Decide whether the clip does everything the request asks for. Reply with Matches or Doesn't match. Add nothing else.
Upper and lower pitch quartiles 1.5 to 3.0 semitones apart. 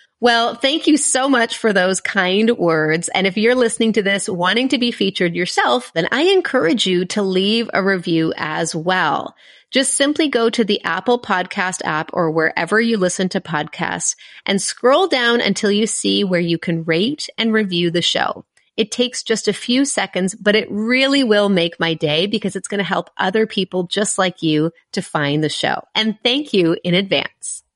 Doesn't match